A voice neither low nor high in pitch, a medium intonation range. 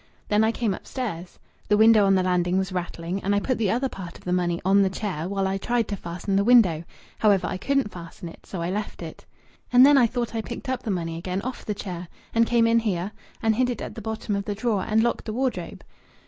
No: high, 205 Hz; average, 3.9 semitones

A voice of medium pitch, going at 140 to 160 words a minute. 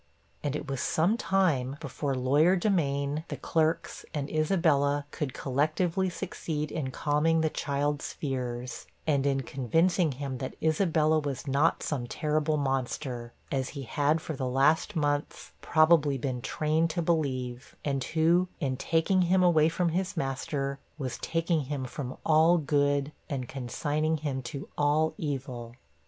Yes: medium, 145 Hz; average, 145 wpm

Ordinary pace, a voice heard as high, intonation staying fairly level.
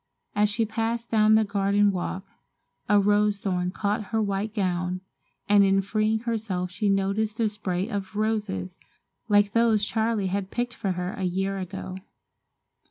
Yes: average, 160 wpm; high, 205 Hz; narrow, 2.2 semitones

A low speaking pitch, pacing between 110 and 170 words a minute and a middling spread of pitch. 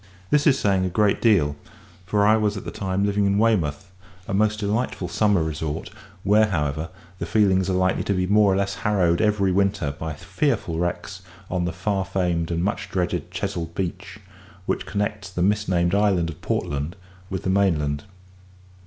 No: very low, 95 Hz; average, 180 wpm; average, 3.0 semitones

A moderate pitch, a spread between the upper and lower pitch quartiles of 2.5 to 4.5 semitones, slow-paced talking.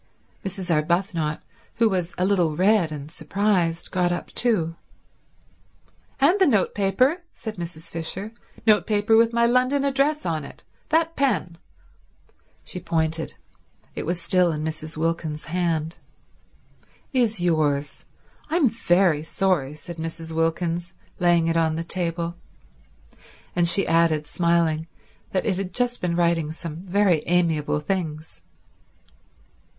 Yes: medium, 175 Hz; average, 3.8 semitones; slow, 125 wpm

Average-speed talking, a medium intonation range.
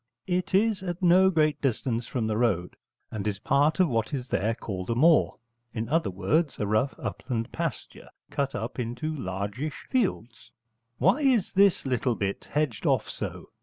No: average, 170 wpm; wide, 7.1 semitones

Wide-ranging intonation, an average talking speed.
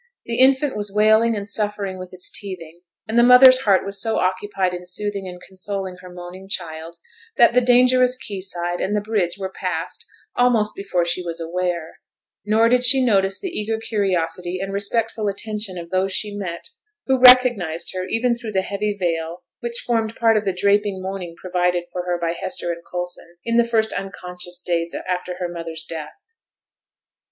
No: average, 3.8 semitones; average, 180 wpm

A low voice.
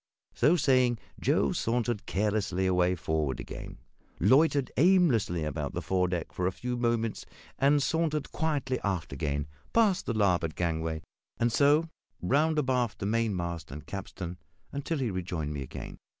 Yes: low, 105 Hz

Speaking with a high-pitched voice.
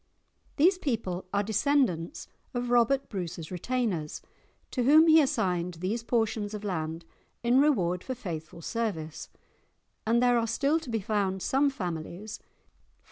Yes: high, 220 Hz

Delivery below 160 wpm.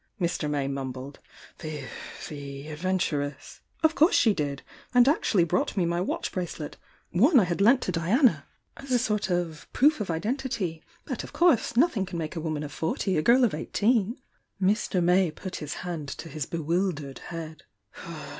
No: average, 175 wpm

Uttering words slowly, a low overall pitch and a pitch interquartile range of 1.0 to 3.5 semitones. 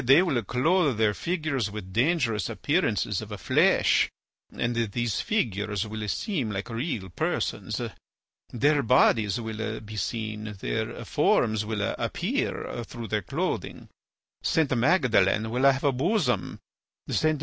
No: slow, 125 wpm; low, 115 Hz; average, 4.5 semitones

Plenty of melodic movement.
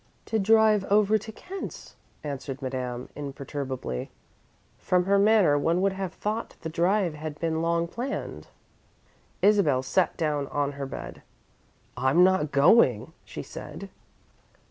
Yes: wide, 6.2 semitones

